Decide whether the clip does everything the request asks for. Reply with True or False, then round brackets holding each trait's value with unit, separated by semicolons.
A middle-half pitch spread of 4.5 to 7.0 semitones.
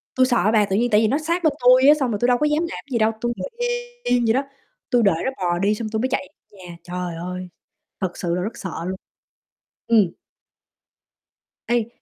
True (5.1 semitones)